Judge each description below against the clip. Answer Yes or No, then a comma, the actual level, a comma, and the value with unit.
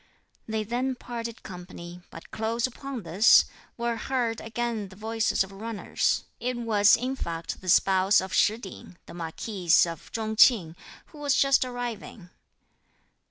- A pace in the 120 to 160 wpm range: Yes, average, 150 wpm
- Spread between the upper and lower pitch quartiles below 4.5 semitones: Yes, average, 4.1 semitones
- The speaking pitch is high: Yes, high, 220 Hz